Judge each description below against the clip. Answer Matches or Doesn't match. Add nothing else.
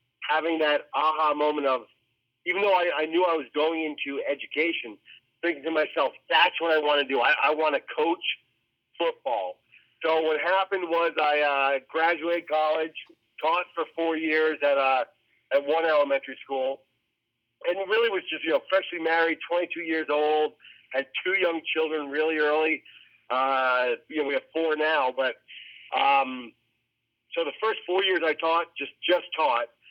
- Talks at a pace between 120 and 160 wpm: Doesn't match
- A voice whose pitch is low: Doesn't match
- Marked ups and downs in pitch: Doesn't match